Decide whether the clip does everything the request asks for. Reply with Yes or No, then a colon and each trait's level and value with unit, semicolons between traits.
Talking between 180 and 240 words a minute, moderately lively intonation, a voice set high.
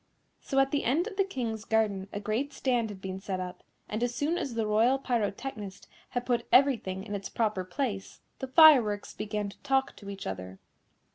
Yes: average, 200 wpm; average, 4.8 semitones; high, 220 Hz